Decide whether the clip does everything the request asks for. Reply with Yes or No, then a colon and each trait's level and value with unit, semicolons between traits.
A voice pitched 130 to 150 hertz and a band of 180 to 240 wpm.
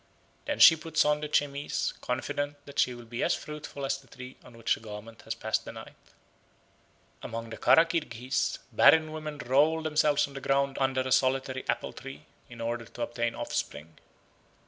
Yes: low, 135 Hz; average, 185 wpm